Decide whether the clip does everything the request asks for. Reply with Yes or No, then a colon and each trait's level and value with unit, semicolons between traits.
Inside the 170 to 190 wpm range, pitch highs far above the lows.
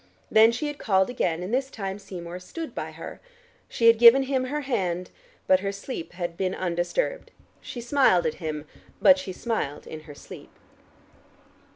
Yes: average, 175 wpm; wide, 6.5 semitones